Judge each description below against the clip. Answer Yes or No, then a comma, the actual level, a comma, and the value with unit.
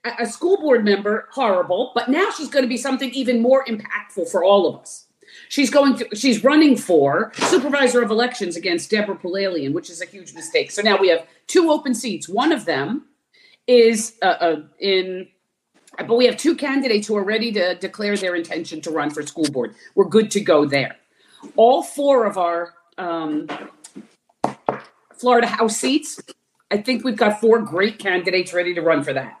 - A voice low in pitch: No, high, 220 Hz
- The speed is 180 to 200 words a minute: Yes, average, 185 wpm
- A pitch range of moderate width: No, wide, 5.8 semitones